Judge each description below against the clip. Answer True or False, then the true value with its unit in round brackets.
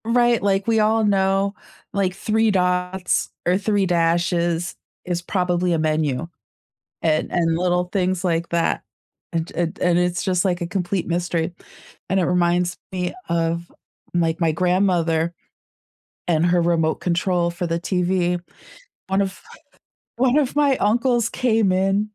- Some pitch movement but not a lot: False (2.3 semitones)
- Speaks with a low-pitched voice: False (180 Hz)